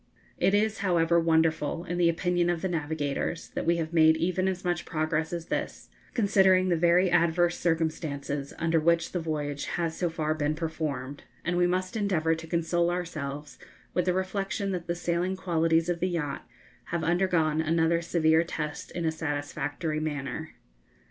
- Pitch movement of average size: No, narrow, 2.0 semitones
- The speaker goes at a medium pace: Yes, average, 170 wpm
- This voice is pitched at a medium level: Yes, medium, 165 Hz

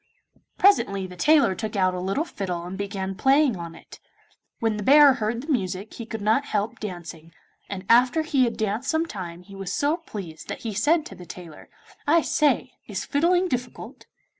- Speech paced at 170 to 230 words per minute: Yes, average, 190 wpm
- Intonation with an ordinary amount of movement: No, wide, 7.1 semitones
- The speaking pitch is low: No, high, 215 Hz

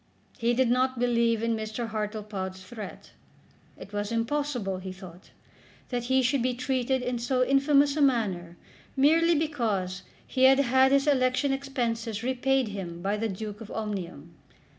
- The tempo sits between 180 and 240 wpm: No, average, 155 wpm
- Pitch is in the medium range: No, high, 235 Hz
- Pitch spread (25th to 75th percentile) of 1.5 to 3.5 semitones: No, average, 4.2 semitones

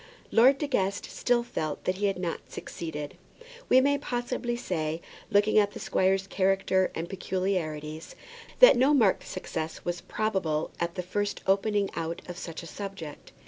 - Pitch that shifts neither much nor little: Yes, average, 4.3 semitones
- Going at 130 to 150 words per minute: No, average, 160 wpm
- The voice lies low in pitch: No, high, 190 Hz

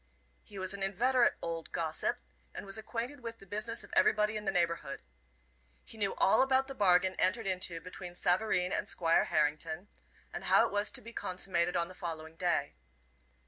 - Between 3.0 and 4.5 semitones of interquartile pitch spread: Yes, average, 4.0 semitones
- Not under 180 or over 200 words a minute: Yes, average, 185 wpm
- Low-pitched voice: No, high, 190 Hz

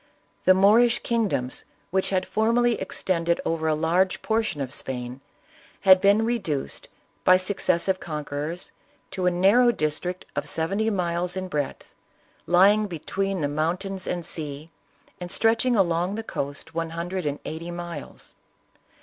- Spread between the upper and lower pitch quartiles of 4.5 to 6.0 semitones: No, average, 3.5 semitones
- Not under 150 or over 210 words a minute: No, average, 140 wpm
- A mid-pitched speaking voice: Yes, medium, 180 Hz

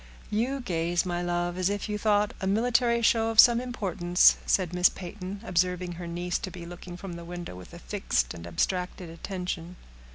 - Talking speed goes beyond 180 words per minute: Yes, average, 190 wpm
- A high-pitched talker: No, medium, 180 Hz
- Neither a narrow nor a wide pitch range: Yes, average, 3.0 semitones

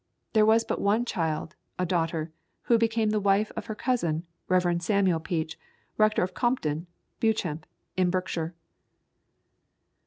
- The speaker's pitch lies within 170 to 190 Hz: Yes, medium, 185 Hz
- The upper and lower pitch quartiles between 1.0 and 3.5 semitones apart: No, average, 4.7 semitones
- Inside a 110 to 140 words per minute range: Yes, slow, 135 wpm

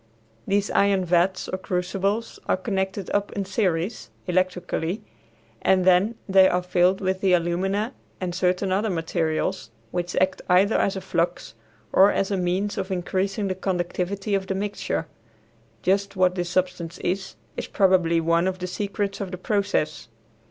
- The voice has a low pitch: No, medium, 185 Hz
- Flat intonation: Yes, narrow, 1.7 semitones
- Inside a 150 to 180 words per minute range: Yes, average, 160 wpm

